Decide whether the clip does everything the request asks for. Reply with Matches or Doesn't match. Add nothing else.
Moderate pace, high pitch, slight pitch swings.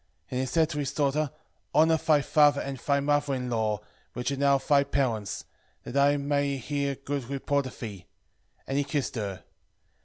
Doesn't match